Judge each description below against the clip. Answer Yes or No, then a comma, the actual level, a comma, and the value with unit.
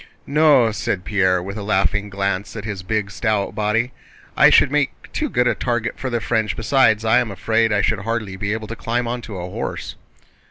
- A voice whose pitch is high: No, low, 110 Hz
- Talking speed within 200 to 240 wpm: Yes, fast, 205 wpm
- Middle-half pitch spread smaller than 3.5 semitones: Yes, average, 2.9 semitones